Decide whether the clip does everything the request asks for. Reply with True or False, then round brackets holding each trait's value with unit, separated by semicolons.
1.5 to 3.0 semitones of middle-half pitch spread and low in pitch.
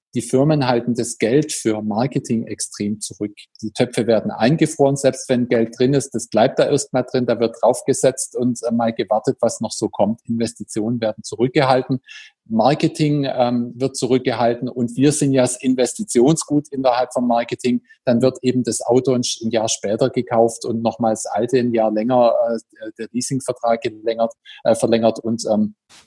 True (2.4 semitones; 120 Hz)